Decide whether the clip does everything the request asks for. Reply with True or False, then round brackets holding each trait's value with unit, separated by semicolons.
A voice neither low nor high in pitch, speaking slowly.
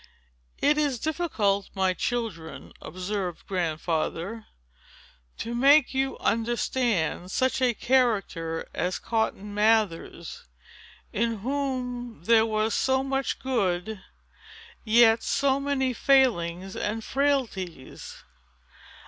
False (225 Hz; 100 wpm)